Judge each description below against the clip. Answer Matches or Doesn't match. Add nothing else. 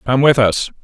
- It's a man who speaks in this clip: Matches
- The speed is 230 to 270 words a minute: Doesn't match